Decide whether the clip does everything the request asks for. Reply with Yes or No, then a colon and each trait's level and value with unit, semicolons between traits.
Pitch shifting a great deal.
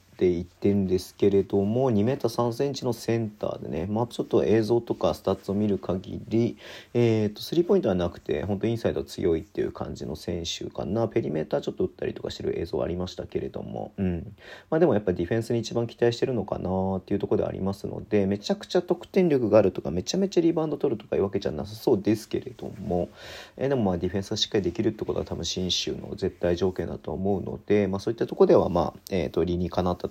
No: average, 4.2 semitones